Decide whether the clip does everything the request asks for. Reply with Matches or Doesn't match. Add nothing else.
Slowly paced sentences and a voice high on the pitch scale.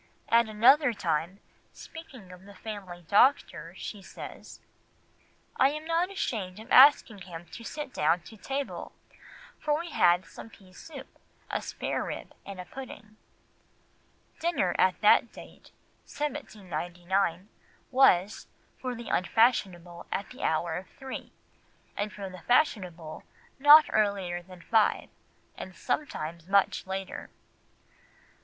Matches